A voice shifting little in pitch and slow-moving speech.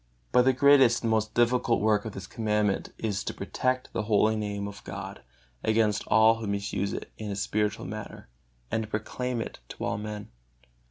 No: narrow, 1.8 semitones; average, 185 wpm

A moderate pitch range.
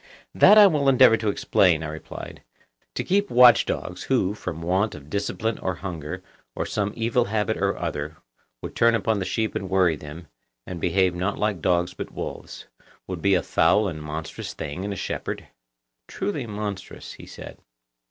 Yes: average, 4.4 semitones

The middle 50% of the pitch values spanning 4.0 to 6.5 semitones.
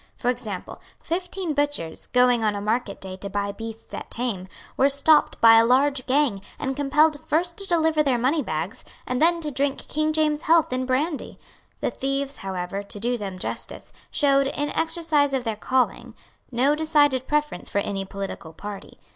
Yes: wide, 5.5 semitones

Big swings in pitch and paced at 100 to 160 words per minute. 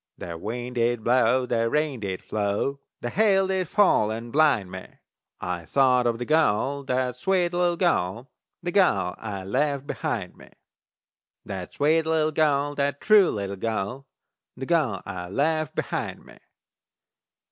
Yes: wide, 6.5 semitones; average, 150 wpm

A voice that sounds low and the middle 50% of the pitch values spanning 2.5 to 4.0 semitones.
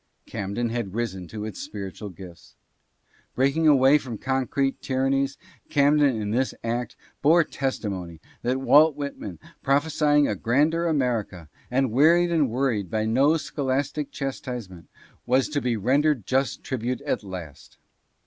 No: low, 130 Hz; average, 4.7 semitones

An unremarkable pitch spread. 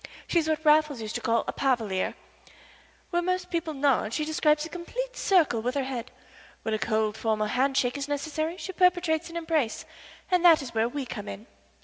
No: wide, 6.1 semitones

